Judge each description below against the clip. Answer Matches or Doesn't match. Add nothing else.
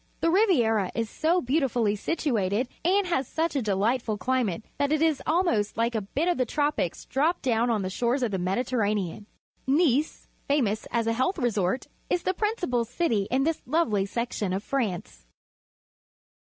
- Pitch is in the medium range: Doesn't match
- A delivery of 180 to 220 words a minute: Doesn't match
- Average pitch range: Doesn't match